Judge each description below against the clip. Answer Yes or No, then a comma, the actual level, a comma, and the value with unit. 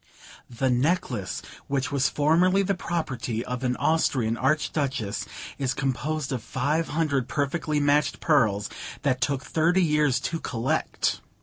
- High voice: No, medium, 140 Hz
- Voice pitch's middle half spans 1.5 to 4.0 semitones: Yes, average, 3.7 semitones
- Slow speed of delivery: Yes, slow, 130 wpm